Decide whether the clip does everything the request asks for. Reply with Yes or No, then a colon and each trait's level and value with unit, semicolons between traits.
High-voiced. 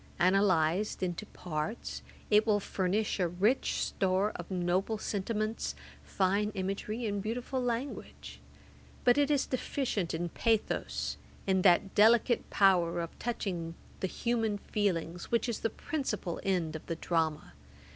Yes: high, 200 Hz